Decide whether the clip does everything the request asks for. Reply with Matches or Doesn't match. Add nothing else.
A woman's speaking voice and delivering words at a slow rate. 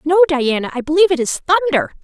Doesn't match